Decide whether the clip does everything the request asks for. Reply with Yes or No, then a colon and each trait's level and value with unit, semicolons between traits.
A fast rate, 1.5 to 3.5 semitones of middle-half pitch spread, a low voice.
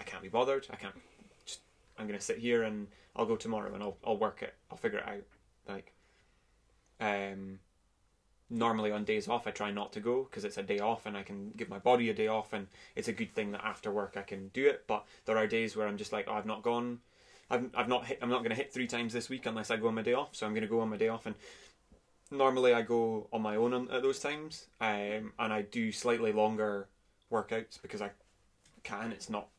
Yes: fast, 245 wpm; narrow, 2.4 semitones; low, 110 Hz